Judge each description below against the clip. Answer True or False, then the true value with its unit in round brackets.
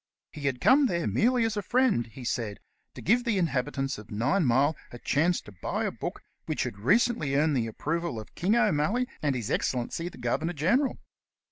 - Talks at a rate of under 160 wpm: False (195 wpm)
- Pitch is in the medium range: True (150 Hz)